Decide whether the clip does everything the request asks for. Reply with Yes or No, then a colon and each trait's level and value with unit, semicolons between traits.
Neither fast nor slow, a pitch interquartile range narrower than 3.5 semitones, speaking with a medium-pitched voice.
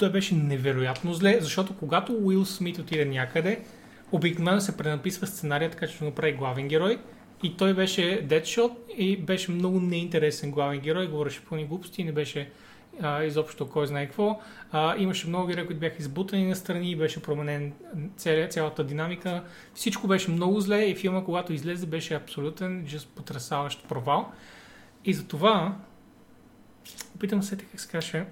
No: average, 155 wpm; average, 4.0 semitones; medium, 175 Hz